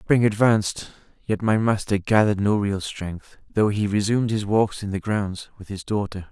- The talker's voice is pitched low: Yes, low, 105 Hz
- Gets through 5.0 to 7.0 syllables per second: No, 4.8 syllables/s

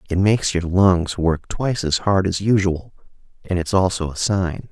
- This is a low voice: Yes, very low, 90 Hz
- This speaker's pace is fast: No, average, 190 wpm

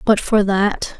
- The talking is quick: No, average, 180 wpm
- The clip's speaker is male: No, female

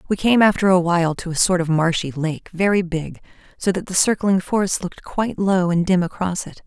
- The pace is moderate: No, fast, 225 wpm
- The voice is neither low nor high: Yes, medium, 180 Hz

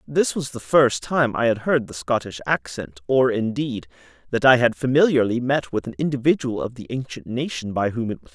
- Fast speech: Yes, fast, 215 wpm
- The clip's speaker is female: No, male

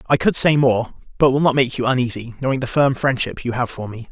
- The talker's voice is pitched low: Yes, low, 130 Hz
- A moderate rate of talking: No, fast, 265 wpm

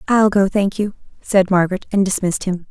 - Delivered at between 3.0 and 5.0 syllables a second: No, 5.8 syllables/s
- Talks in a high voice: Yes, high, 195 Hz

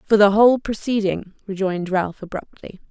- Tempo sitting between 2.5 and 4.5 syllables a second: No, 5.4 syllables/s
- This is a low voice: No, high, 200 Hz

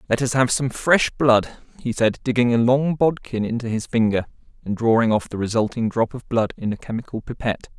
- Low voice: Yes, low, 120 Hz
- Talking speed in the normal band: No, fast, 210 wpm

